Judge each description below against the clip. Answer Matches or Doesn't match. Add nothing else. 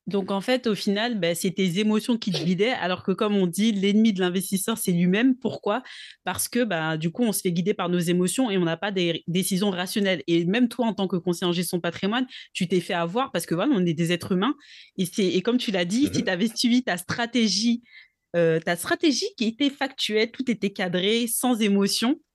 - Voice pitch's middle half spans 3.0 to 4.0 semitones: Doesn't match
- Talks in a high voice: Matches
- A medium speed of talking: Doesn't match